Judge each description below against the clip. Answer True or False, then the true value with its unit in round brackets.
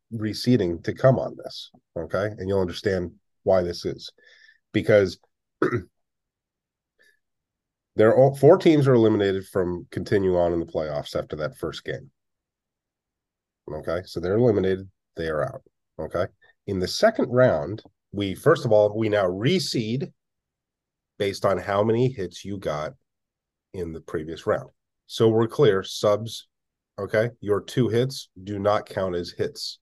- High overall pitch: False (105 Hz)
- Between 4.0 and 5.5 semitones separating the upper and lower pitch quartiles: True (5.0 semitones)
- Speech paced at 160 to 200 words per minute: False (145 wpm)